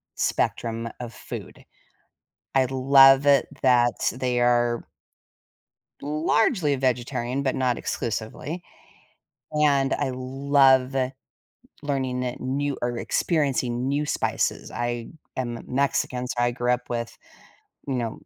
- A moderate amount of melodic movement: No, narrow, 2.3 semitones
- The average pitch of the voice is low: Yes, low, 130 Hz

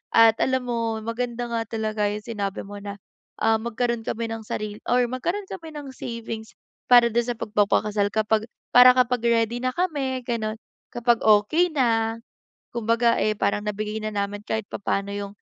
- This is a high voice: Yes, high, 225 Hz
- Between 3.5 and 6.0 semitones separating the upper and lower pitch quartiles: No, narrow, 2.4 semitones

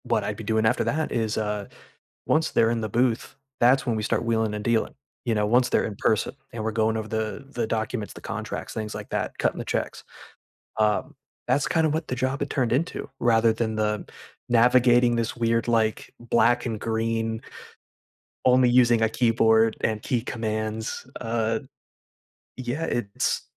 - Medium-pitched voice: No, low, 115 Hz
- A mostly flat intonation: Yes, narrow, 1.8 semitones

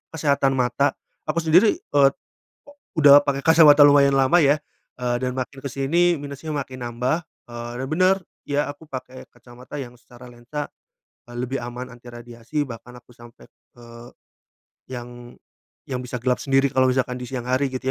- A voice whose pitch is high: No, low, 130 Hz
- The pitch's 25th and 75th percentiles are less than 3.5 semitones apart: Yes, average, 2.9 semitones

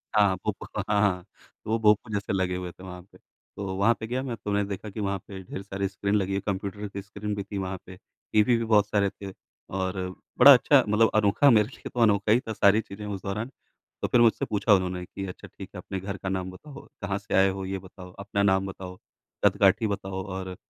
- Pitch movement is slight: Yes, narrow, 1.7 semitones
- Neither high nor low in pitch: No, low, 100 Hz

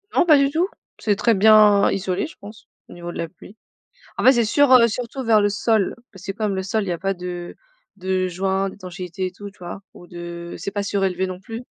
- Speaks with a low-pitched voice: No, high, 195 Hz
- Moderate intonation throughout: Yes, average, 3.1 semitones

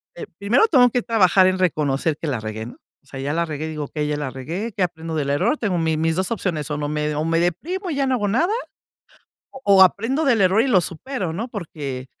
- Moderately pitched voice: Yes, medium, 170 Hz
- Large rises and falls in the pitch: Yes, wide, 6.7 semitones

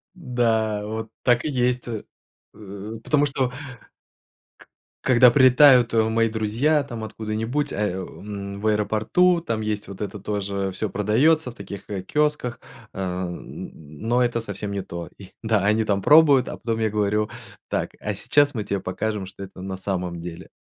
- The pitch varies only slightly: No, average, 3.7 semitones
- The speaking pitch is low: Yes, low, 110 Hz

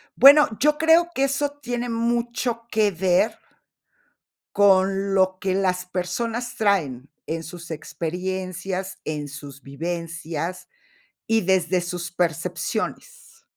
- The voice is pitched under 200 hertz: Yes, high, 190 Hz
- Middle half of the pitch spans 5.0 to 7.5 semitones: Yes, average, 5.3 semitones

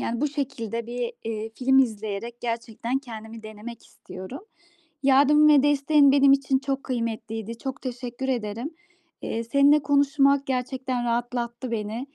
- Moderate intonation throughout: Yes, average, 3.1 semitones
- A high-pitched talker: Yes, high, 245 Hz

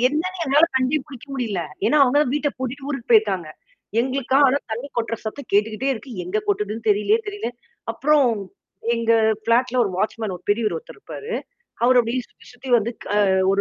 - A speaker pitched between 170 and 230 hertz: No, high, 245 Hz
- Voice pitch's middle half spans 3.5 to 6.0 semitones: Yes, average, 4.0 semitones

